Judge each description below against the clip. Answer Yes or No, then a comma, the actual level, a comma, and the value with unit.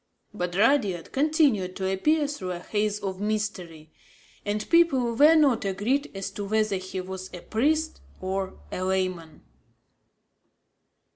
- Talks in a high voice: Yes, high, 205 Hz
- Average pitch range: No, wide, 5.9 semitones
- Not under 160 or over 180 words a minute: No, slow, 135 wpm